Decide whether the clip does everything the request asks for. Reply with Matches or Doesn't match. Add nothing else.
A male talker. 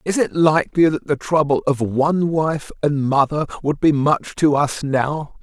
Matches